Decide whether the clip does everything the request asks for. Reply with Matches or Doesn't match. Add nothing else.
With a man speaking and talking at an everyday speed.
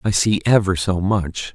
Matches